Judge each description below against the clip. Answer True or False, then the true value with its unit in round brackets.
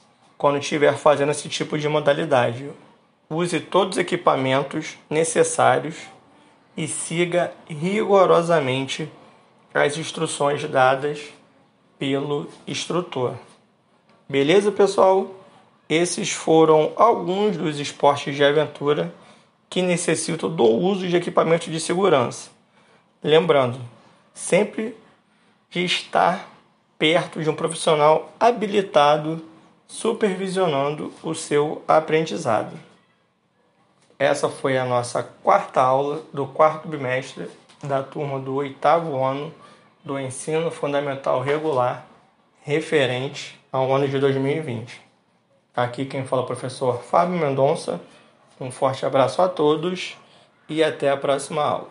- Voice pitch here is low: False (155 Hz)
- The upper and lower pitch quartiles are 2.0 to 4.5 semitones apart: True (3.9 semitones)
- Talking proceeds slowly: True (105 wpm)